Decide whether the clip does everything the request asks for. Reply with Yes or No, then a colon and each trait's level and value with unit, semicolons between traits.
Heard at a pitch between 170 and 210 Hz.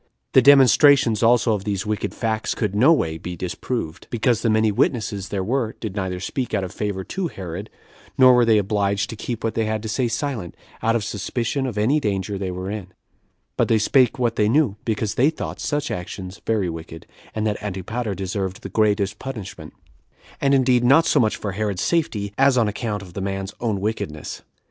No: low, 110 Hz